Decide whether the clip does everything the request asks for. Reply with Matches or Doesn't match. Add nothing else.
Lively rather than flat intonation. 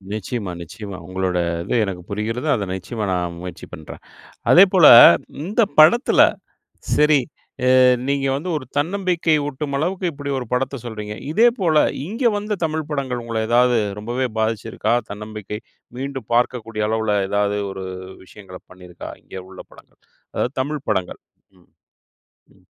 Matches